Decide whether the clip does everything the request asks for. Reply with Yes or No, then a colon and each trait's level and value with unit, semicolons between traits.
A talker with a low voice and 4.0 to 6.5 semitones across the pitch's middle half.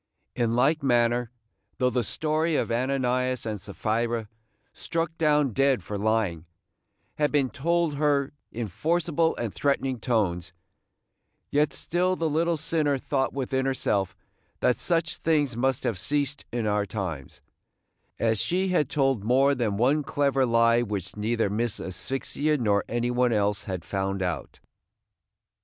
Yes: low, 125 Hz; average, 5.1 semitones